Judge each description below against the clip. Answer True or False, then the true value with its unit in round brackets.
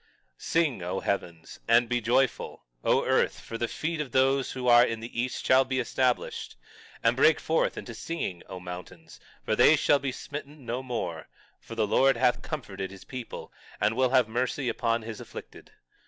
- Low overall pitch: True (120 Hz)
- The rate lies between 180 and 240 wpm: True (185 wpm)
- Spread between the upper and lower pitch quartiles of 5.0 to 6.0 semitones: False (3.0 semitones)